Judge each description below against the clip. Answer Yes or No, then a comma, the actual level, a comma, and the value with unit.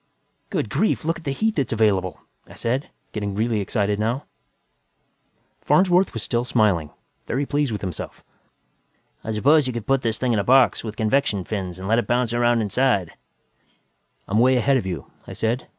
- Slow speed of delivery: No, average, 185 wpm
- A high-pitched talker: No, low, 115 Hz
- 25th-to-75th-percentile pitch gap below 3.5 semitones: No, average, 4.2 semitones